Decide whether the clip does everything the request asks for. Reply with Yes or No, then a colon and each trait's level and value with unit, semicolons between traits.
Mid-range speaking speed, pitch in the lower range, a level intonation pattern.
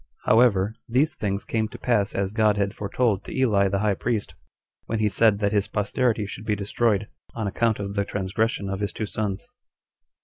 Yes: average, 195 wpm; low, 105 Hz; narrow, 2.0 semitones